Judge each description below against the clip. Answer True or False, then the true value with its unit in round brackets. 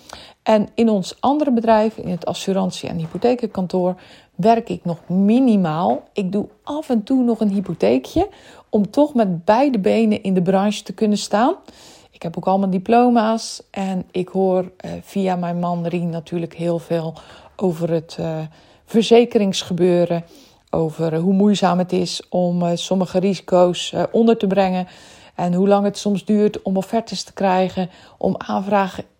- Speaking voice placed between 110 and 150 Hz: False (190 Hz)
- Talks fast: False (150 wpm)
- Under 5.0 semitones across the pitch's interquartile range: True (3.5 semitones)